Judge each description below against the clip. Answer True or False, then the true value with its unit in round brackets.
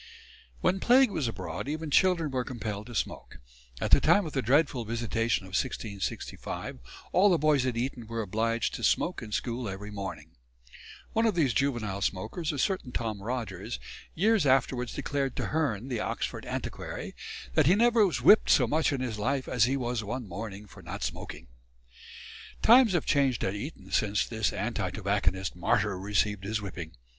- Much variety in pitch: True (5.9 semitones)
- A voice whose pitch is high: False (120 Hz)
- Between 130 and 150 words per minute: False (175 wpm)